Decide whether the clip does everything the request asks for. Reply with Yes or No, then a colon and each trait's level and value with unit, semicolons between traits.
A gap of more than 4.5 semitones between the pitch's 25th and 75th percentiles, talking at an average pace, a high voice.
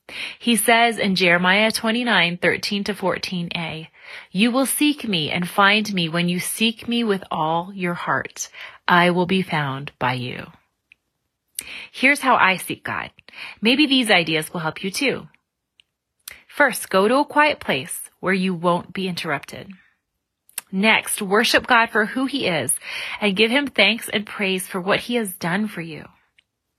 Yes: average, 4.9 semitones; average, 165 wpm; high, 195 Hz